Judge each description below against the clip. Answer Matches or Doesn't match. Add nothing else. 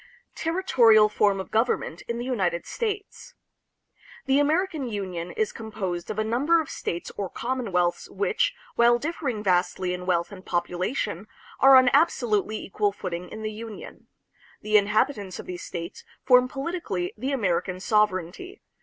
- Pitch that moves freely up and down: Matches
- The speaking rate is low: Doesn't match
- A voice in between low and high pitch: Doesn't match